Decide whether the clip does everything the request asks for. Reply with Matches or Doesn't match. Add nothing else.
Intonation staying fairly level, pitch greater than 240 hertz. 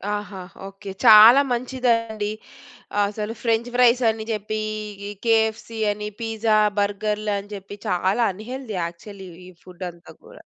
Doesn't match